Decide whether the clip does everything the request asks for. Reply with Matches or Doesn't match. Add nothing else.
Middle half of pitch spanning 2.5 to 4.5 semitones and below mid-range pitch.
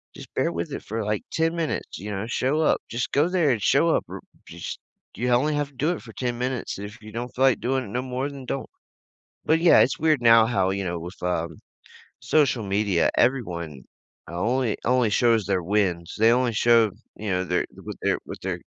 Doesn't match